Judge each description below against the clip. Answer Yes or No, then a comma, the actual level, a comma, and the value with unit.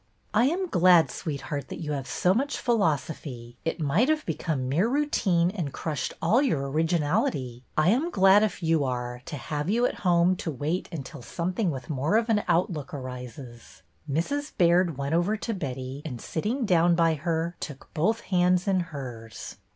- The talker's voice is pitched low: No, medium, 165 Hz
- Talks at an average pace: Yes, average, 180 wpm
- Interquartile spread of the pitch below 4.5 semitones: No, wide, 5.4 semitones